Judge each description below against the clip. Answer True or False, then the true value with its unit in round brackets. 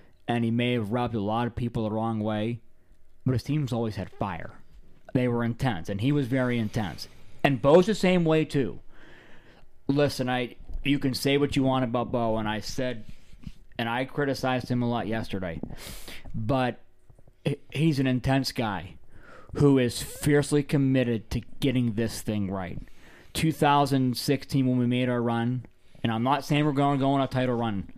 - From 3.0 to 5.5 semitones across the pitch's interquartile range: True (3.6 semitones)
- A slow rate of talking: False (180 wpm)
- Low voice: True (125 Hz)